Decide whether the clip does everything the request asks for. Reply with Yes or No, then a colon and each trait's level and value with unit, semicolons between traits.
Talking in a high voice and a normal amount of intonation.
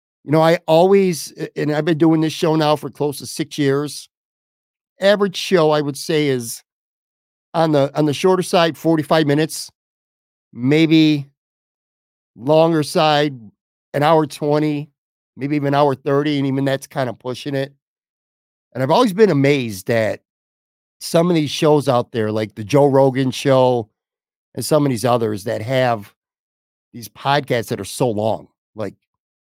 No: medium, 140 Hz; average, 4.4 semitones